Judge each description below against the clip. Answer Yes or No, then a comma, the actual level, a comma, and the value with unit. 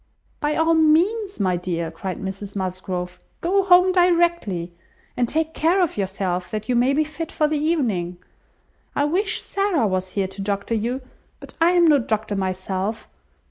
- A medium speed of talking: Yes, average, 170 wpm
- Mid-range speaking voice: No, high, 235 Hz